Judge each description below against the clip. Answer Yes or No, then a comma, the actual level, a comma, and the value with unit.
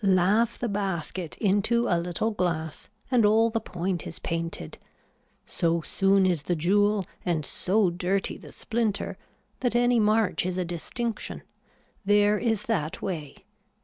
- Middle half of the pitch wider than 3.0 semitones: Yes, average, 4.1 semitones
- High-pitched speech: Yes, high, 195 Hz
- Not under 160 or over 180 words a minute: No, average, 145 wpm